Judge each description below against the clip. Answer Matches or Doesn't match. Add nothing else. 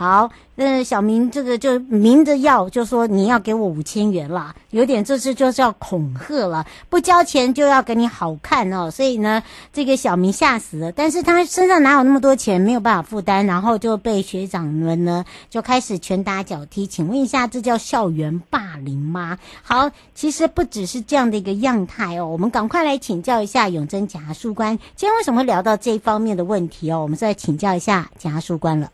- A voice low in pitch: Doesn't match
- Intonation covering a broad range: Matches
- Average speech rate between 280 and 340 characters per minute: Matches